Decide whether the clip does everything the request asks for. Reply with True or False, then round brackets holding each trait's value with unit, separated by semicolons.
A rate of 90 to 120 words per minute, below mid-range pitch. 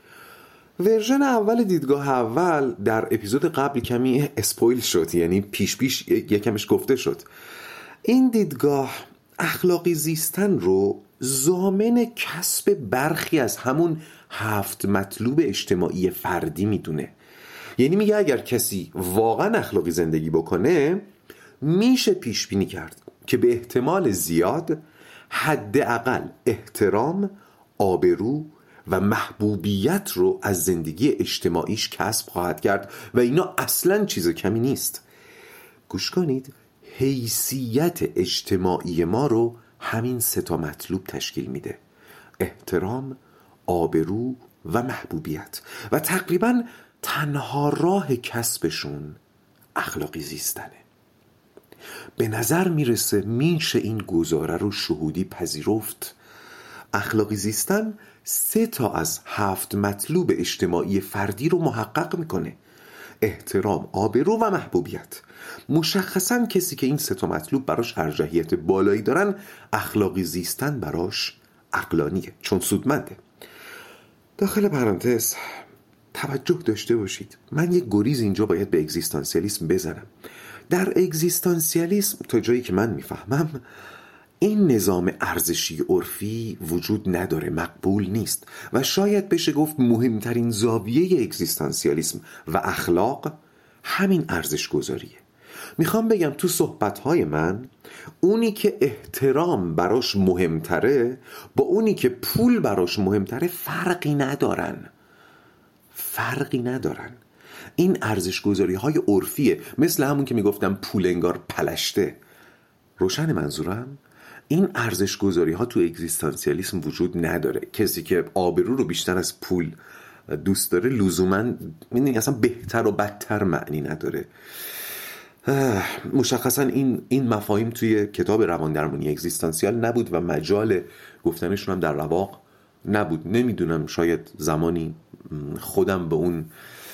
True (110 wpm; 125 Hz)